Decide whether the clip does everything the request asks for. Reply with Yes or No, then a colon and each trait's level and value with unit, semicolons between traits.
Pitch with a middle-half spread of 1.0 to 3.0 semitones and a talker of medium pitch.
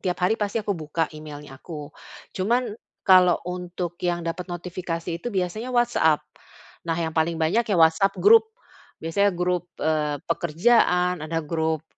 Yes: average, 2.7 semitones; medium, 175 Hz